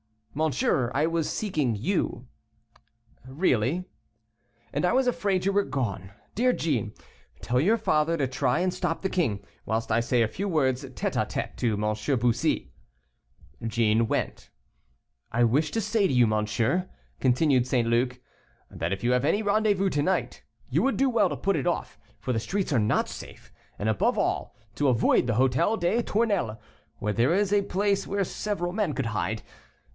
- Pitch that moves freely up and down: Yes, wide, 8.5 semitones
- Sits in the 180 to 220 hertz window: No, medium, 140 Hz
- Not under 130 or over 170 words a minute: No, average, 180 wpm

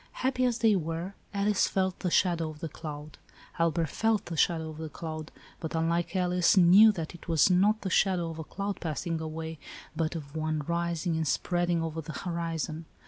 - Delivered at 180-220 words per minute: Yes, average, 195 wpm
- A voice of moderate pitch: Yes, medium, 170 Hz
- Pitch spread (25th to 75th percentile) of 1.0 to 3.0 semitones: Yes, narrow, 2.4 semitones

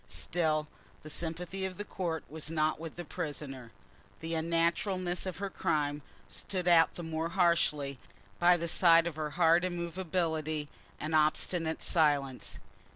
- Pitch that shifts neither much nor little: No, narrow, 2.3 semitones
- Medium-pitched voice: Yes, medium, 165 Hz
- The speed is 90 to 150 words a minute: Yes, average, 145 wpm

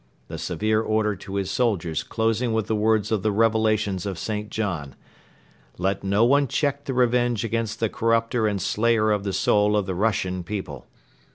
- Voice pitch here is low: Yes, low, 110 Hz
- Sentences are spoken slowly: No, average, 180 wpm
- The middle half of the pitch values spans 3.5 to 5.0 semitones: No, narrow, 2.4 semitones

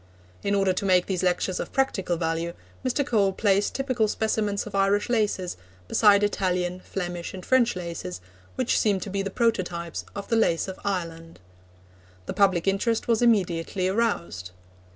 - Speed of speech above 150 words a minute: Yes, average, 160 wpm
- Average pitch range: Yes, average, 3.3 semitones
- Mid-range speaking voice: No, high, 195 Hz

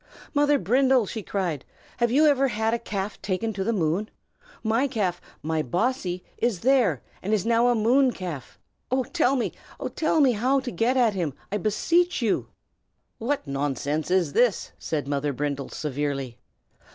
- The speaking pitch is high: Yes, high, 215 Hz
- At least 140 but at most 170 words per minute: Yes, average, 165 wpm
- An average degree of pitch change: No, wide, 7.6 semitones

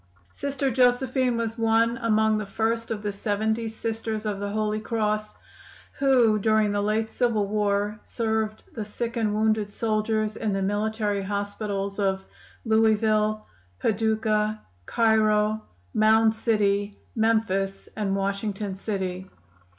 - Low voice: No, high, 215 Hz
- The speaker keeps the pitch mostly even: Yes, narrow, 1.4 semitones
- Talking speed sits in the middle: No, slow, 125 wpm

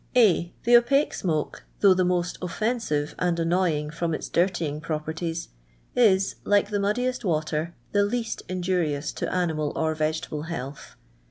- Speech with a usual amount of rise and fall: Yes, average, 4.4 semitones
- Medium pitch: Yes, medium, 175 Hz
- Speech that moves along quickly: No, average, 150 wpm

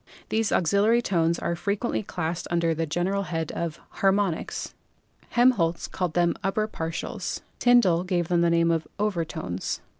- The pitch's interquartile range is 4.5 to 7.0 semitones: No, average, 3.3 semitones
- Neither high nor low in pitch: Yes, medium, 175 Hz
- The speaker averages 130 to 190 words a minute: Yes, average, 150 wpm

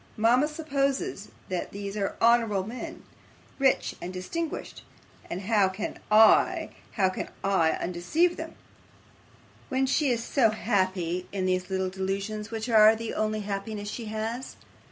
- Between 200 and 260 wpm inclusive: No, average, 140 wpm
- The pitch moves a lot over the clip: No, average, 3.9 semitones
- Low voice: No, high, 215 Hz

